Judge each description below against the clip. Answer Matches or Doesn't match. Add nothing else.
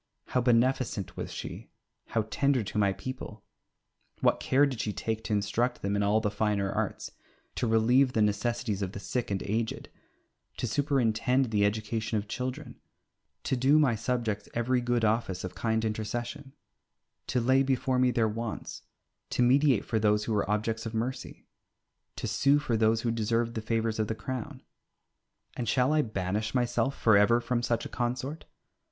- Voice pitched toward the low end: Matches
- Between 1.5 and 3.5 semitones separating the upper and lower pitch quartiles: Matches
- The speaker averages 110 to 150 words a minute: Doesn't match